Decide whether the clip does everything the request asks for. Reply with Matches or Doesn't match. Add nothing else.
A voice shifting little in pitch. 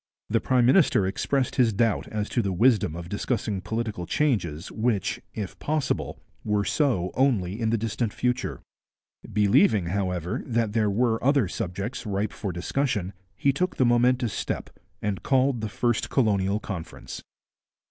Doesn't match